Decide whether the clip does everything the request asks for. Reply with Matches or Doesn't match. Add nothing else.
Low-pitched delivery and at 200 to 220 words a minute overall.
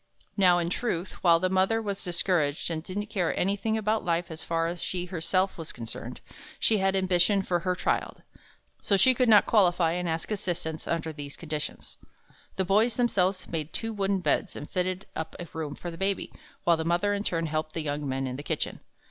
Doesn't match